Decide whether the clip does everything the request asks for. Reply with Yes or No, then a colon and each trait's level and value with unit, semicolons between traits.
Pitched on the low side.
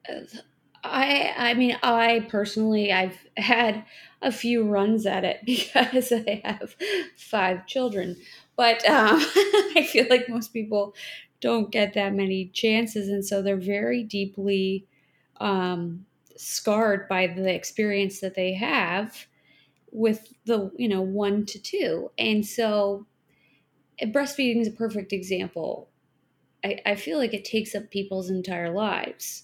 No: high, 210 Hz